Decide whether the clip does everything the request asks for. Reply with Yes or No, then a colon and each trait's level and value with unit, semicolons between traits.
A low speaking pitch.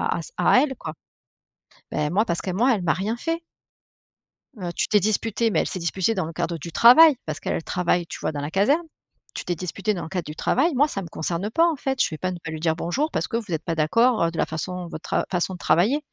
No: medium, 185 Hz